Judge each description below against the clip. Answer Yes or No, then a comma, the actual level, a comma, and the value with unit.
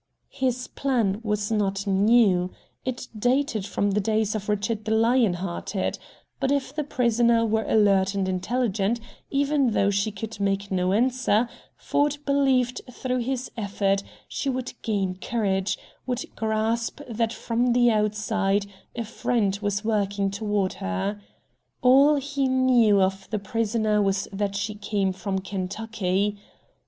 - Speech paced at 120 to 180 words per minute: Yes, average, 140 wpm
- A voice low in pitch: No, high, 215 Hz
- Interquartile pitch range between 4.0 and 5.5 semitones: No, average, 3.5 semitones